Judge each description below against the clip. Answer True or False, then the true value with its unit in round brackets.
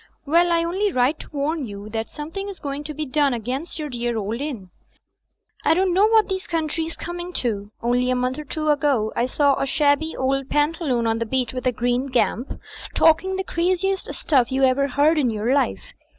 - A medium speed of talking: False (210 wpm)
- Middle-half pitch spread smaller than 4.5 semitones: False (4.9 semitones)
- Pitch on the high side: True (280 Hz)